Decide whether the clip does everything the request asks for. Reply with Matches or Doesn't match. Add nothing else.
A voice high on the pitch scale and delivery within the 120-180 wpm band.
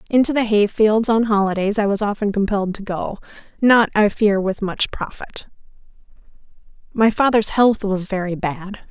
Matches